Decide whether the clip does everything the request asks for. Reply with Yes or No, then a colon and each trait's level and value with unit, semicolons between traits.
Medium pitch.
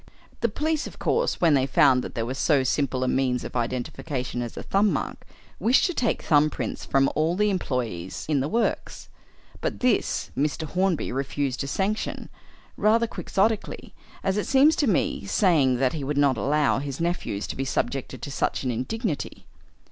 Yes: medium, 145 Hz